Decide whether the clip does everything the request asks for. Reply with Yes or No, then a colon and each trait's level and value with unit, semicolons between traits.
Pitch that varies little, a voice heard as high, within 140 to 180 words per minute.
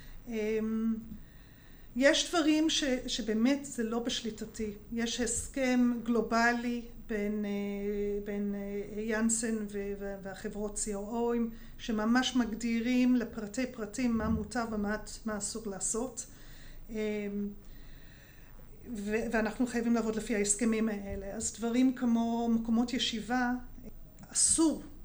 No: narrow, 2.3 semitones; high, 225 Hz; slow, 100 wpm